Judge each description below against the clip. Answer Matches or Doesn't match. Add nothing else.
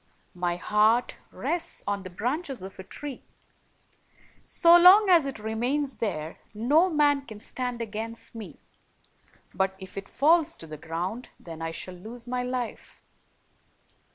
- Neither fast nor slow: Matches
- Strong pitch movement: Matches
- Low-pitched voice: Doesn't match